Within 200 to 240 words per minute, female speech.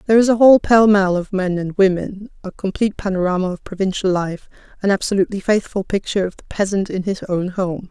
Yes: fast, 205 wpm; female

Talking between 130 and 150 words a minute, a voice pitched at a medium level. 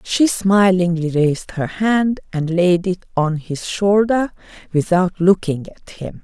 Yes: average, 145 wpm; medium, 180 Hz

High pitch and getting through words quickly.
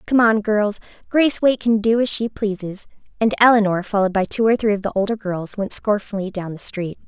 Yes: high, 210 Hz; fast, 220 wpm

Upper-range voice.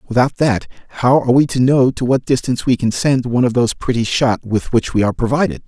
No: low, 125 Hz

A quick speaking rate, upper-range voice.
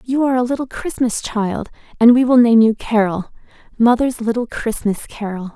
No: average, 160 wpm; high, 235 Hz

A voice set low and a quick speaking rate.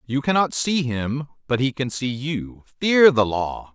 No: low, 130 Hz; average, 190 wpm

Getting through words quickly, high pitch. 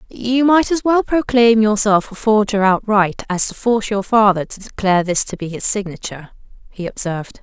No: average, 185 wpm; high, 210 Hz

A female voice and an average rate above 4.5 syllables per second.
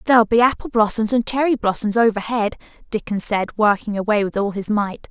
Yes: female; 5.7 syllables/s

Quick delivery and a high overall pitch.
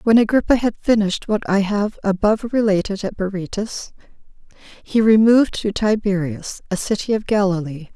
No: average, 145 wpm; high, 205 Hz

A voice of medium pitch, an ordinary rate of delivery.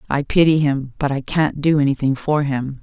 No: medium, 145 Hz; fast, 210 wpm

